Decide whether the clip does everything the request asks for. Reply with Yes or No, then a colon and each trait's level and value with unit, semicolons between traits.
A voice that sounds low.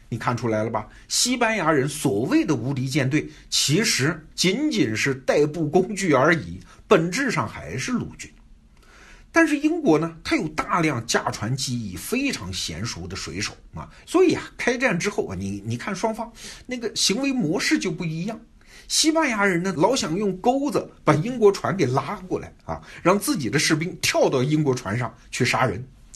No: medium, 155 Hz